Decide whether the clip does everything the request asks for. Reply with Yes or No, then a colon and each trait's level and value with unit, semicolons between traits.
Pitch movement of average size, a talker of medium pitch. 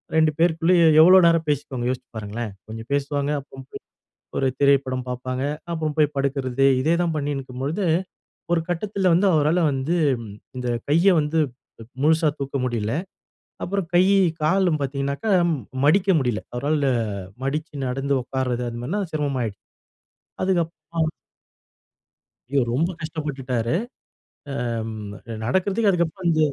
Yes: average, 4.3 semitones; medium, 145 Hz